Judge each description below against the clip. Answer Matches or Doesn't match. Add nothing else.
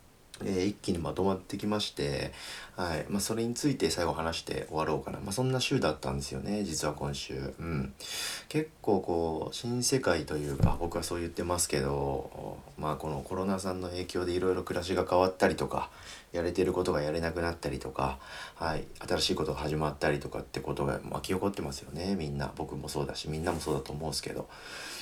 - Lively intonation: Doesn't match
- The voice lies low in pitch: Matches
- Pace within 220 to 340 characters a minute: Doesn't match